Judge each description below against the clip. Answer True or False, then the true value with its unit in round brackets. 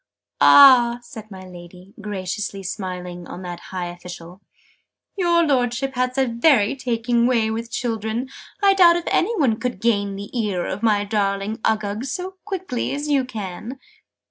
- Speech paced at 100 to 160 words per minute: True (155 wpm)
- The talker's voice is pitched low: False (225 Hz)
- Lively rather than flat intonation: False (4.7 semitones)